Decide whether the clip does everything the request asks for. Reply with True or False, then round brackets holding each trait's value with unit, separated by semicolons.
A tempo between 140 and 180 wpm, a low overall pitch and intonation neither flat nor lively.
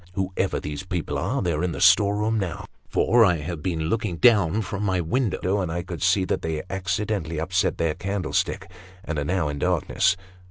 False (195 wpm; 90 Hz; 3.4 semitones)